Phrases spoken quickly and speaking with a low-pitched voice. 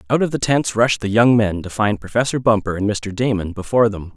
Yes: fast, 245 wpm; low, 110 Hz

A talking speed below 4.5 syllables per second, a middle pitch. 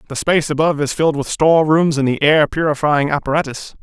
No: 6.5 syllables/s; medium, 150 Hz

